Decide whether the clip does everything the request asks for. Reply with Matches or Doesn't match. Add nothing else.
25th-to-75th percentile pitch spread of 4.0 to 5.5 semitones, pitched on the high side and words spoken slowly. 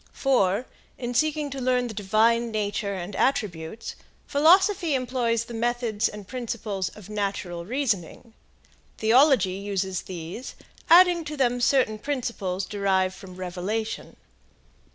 Matches